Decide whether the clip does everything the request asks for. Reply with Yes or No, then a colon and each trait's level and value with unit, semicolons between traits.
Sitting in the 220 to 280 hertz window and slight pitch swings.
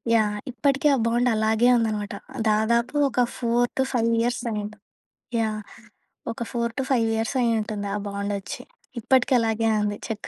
Yes: high, 225 Hz; narrow, 2.3 semitones